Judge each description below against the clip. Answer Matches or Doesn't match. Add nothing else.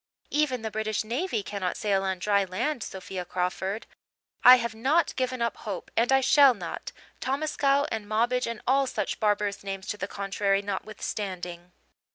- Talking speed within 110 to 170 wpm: Matches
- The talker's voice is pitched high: Matches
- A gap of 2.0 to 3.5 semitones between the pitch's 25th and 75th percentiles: Doesn't match